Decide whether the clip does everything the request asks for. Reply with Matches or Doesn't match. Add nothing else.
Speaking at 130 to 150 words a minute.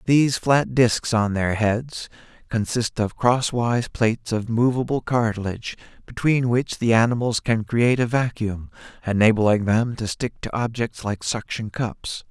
Matches